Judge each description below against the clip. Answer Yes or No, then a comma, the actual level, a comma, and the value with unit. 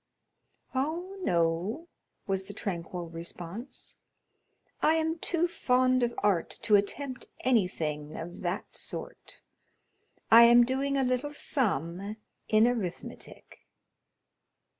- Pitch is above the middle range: Yes, high, 225 Hz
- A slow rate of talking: Yes, slow, 105 wpm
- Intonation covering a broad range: Yes, wide, 7.1 semitones